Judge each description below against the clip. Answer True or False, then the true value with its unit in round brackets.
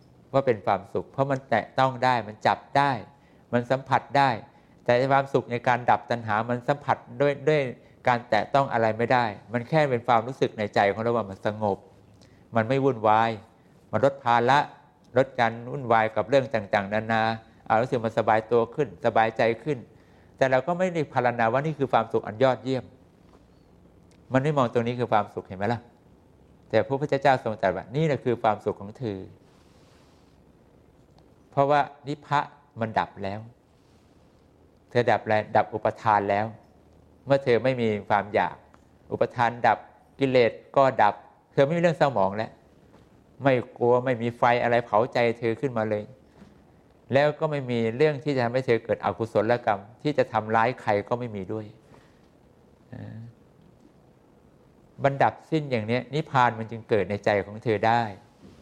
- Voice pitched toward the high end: False (120 Hz)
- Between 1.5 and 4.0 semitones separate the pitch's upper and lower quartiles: True (3.4 semitones)